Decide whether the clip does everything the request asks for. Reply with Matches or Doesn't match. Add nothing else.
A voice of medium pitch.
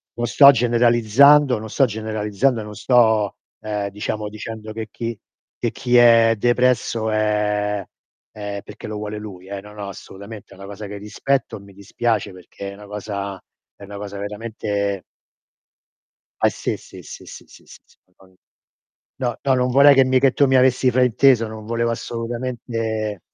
Doesn't match